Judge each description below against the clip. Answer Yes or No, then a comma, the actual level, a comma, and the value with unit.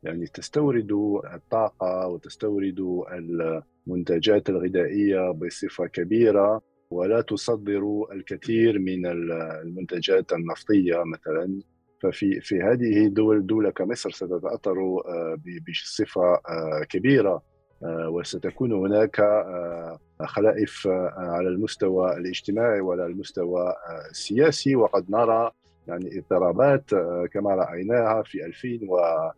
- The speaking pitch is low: Yes, very low, 90 Hz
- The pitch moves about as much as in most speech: Yes, average, 3.7 semitones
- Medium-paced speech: Yes, average, 85 wpm